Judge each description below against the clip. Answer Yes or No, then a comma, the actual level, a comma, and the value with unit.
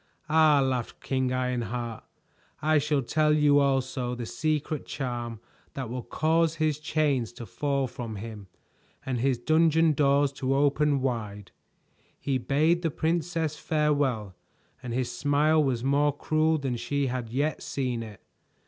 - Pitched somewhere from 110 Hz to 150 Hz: Yes, medium, 140 Hz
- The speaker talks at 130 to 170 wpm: Yes, average, 145 wpm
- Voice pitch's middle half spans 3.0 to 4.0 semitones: Yes, average, 3.6 semitones